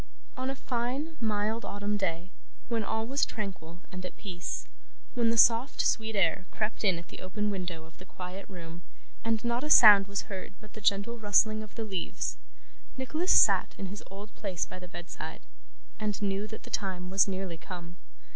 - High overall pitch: Yes, high, 205 Hz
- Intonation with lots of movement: No, average, 3.3 semitones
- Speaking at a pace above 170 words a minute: Yes, average, 190 wpm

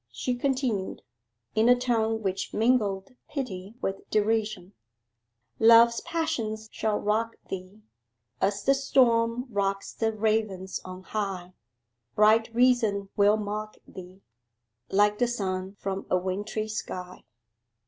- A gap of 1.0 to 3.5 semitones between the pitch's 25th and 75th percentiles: Yes, average, 2.9 semitones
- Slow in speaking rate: Yes, slow, 115 wpm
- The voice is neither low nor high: No, high, 215 Hz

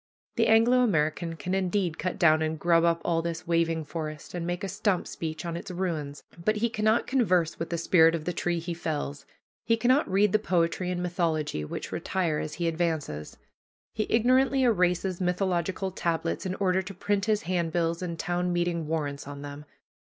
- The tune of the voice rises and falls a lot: No, average, 2.7 semitones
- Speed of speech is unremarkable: Yes, average, 190 wpm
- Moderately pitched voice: Yes, medium, 175 Hz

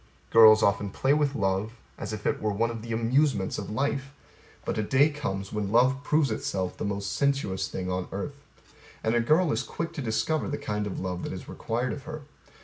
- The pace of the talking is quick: Yes, fast, 215 wpm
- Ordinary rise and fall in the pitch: No, wide, 5.7 semitones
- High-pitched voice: No, low, 115 Hz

